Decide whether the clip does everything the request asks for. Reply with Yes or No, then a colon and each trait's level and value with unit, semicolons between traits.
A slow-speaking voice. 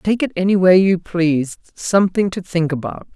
No: average, 190 wpm